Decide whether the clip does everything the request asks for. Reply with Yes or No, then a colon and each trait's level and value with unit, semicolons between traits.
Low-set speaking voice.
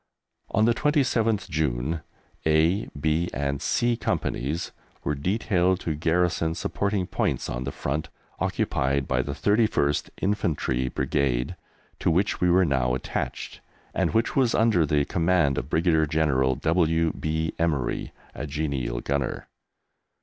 Yes: very low, 80 Hz